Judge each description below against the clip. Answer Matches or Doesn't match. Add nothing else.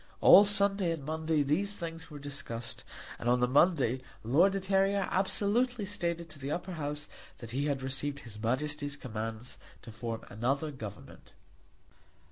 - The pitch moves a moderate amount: Doesn't match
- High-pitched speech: Doesn't match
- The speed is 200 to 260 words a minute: Doesn't match